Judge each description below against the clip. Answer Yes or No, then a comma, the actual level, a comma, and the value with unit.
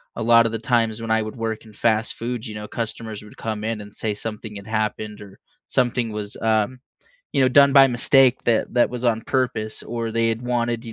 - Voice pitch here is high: No, low, 115 Hz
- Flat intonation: Yes, narrow, 1.8 semitones